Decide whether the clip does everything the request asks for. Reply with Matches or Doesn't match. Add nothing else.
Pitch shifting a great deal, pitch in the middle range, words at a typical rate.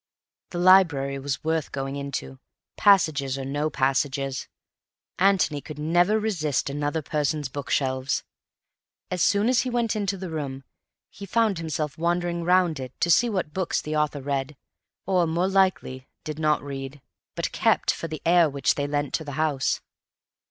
Doesn't match